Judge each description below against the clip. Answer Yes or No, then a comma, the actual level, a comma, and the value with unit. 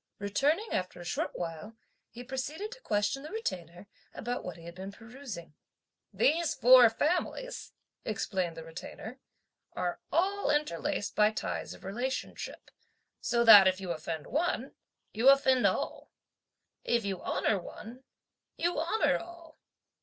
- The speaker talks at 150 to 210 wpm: No, average, 140 wpm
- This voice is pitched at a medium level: No, high, 235 Hz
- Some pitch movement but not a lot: No, wide, 7.9 semitones